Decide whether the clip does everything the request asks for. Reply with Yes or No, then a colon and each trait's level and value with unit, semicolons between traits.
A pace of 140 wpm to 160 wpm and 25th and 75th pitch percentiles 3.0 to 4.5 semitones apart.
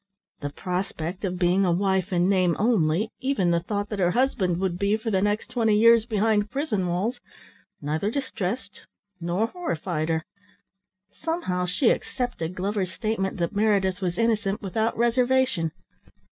Yes: average, 150 wpm; average, 3.9 semitones